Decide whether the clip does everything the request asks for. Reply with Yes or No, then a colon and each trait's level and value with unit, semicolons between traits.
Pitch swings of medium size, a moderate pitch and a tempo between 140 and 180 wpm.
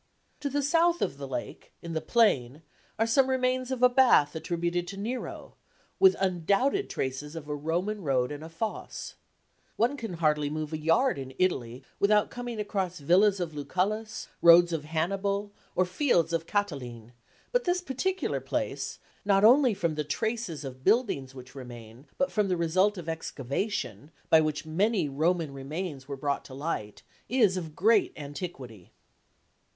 No: wide, 6.7 semitones; medium, 175 Hz; average, 165 wpm